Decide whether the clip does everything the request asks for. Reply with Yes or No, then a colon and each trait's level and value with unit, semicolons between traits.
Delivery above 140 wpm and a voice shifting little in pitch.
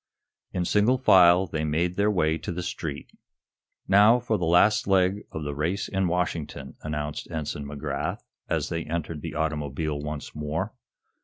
No: average, 160 wpm; average, 3.8 semitones